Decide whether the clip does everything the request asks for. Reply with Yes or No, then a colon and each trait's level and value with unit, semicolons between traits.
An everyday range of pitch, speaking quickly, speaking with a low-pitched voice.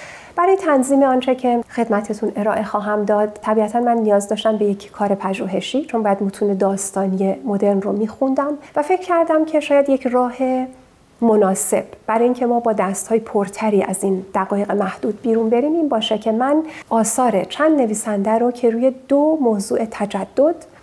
No: average, 4.2 semitones; fast, 165 wpm; high, 225 Hz